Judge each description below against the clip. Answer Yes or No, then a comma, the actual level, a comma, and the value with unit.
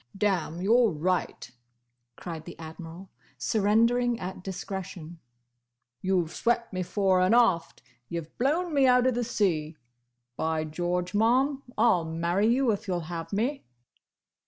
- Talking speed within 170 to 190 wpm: No, average, 145 wpm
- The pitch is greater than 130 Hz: Yes, high, 190 Hz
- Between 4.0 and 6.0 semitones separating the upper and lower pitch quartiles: Yes, wide, 5.5 semitones